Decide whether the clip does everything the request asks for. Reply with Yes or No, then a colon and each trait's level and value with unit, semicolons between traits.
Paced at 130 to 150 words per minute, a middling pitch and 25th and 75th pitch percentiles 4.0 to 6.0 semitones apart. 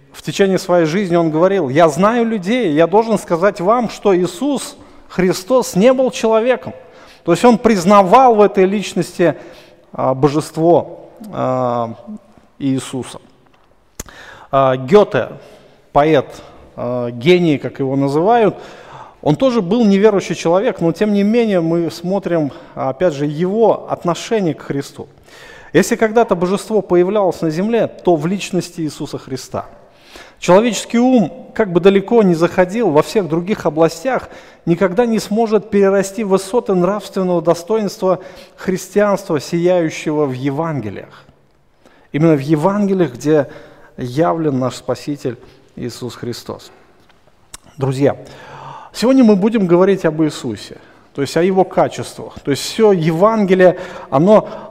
No: average, 120 wpm; medium, 180 Hz; average, 5.2 semitones